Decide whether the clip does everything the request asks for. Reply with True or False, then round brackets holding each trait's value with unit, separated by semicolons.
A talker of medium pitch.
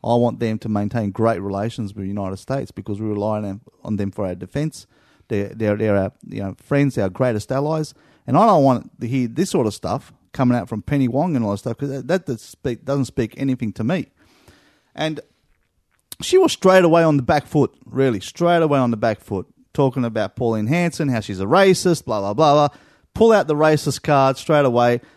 False (125 Hz)